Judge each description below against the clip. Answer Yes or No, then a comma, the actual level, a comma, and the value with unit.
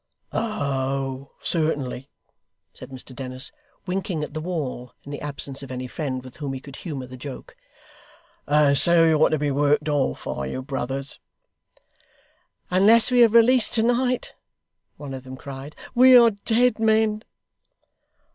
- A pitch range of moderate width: No, wide, 7.8 semitones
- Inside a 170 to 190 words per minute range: No, average, 150 wpm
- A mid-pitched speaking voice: Yes, medium, 145 Hz